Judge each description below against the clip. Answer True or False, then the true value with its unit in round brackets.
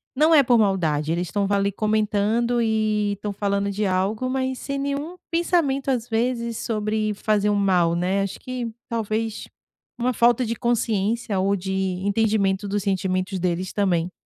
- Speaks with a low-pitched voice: False (210 Hz)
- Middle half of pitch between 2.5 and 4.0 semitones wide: True (3.3 semitones)